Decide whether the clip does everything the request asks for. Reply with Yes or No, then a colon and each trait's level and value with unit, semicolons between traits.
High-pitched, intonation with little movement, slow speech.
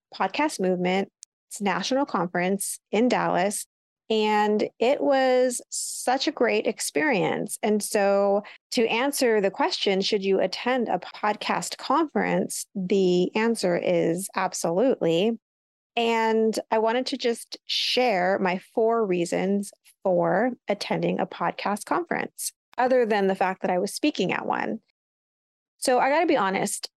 No: high, 215 Hz; average, 4.5 semitones; slow, 130 wpm